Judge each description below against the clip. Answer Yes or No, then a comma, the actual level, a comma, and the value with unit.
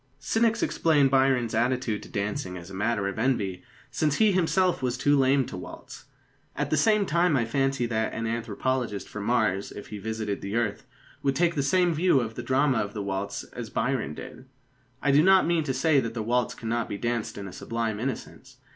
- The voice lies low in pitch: Yes, low, 125 Hz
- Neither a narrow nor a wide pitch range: Yes, average, 4.6 semitones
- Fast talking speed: Yes, fast, 210 wpm